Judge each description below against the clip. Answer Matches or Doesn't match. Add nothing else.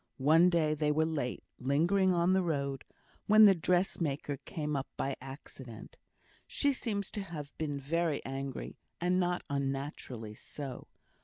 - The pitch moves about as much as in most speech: Matches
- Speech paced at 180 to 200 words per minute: Doesn't match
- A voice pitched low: Doesn't match